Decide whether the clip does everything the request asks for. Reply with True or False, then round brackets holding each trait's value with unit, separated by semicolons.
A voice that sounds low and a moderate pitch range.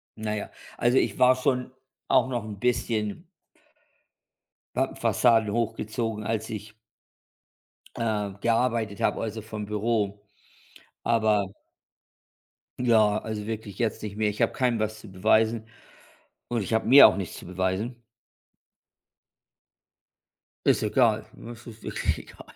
False (110 Hz; 1.9 semitones)